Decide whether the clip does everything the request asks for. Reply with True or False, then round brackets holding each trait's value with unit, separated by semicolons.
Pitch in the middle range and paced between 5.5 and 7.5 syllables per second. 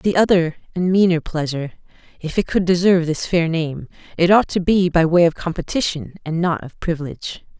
True (170 Hz; 5.6 syllables/s)